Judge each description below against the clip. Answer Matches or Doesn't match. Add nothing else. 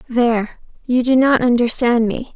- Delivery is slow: Matches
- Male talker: Doesn't match